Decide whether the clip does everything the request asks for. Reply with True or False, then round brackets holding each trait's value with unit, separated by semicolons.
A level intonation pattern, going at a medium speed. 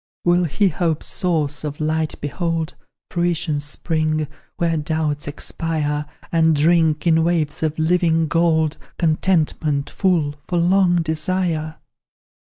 False (2.0 semitones; 115 wpm)